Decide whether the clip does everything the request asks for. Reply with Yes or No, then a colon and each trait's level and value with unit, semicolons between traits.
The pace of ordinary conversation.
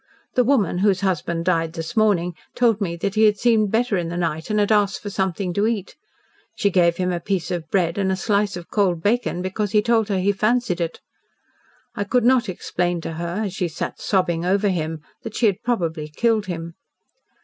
No: fast, 215 wpm